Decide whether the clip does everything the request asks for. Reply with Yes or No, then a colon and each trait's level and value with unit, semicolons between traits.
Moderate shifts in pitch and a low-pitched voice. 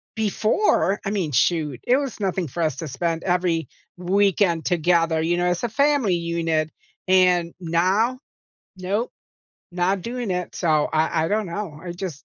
No: average, 3.4 semitones; medium, 180 Hz